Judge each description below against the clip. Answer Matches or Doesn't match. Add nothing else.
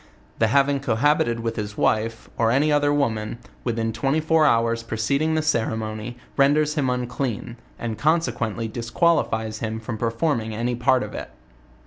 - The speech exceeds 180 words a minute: Doesn't match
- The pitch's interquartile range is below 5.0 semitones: Matches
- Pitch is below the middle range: Matches